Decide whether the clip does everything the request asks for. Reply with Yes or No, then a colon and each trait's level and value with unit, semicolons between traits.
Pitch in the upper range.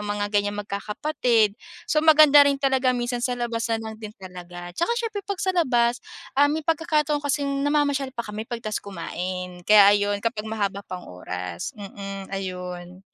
Yes: high, 220 Hz